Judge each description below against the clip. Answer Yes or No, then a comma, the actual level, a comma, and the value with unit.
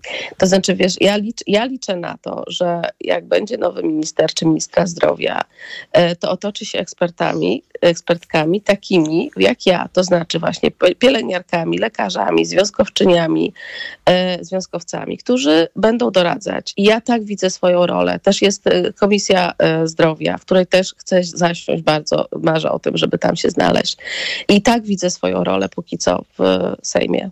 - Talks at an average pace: Yes, average, 145 wpm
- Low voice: No, medium, 185 Hz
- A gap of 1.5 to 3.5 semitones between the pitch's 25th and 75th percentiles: No, average, 4.2 semitones